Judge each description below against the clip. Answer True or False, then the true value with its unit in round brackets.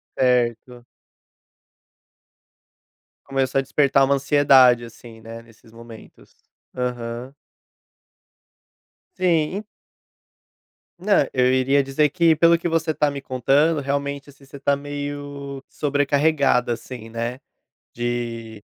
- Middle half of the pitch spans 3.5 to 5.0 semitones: False (3.0 semitones)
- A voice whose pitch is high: False (135 Hz)